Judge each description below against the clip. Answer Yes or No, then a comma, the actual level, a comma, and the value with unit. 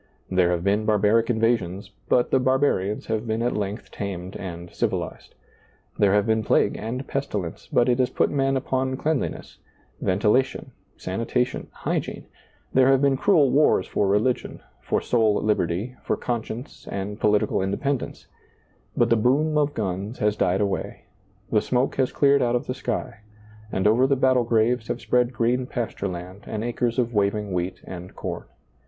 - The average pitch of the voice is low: Yes, low, 115 Hz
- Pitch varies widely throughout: No, average, 4.2 semitones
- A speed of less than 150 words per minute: No, average, 165 wpm